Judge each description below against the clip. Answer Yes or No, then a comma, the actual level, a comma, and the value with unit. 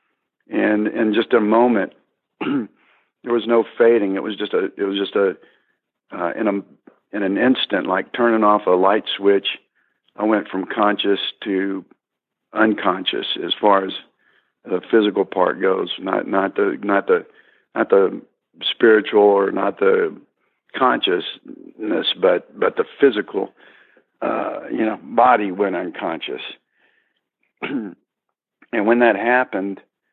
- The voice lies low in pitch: Yes, low, 110 Hz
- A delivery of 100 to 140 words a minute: Yes, slow, 135 wpm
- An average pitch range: Yes, average, 3.8 semitones